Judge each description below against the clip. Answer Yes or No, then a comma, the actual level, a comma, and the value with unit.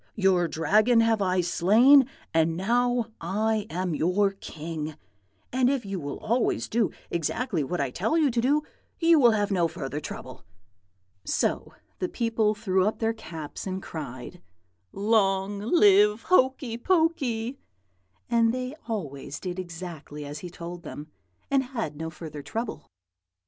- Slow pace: No, average, 145 wpm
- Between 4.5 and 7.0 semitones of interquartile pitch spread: Yes, wide, 5.6 semitones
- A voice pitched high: Yes, high, 200 Hz